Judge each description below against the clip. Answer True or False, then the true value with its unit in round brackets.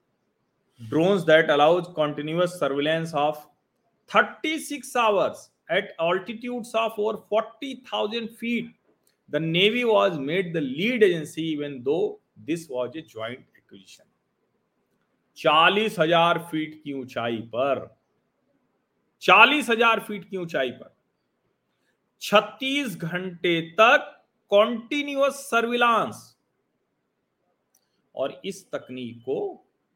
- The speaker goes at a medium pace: False (100 wpm)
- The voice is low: False (190 Hz)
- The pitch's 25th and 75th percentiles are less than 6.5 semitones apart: False (6.8 semitones)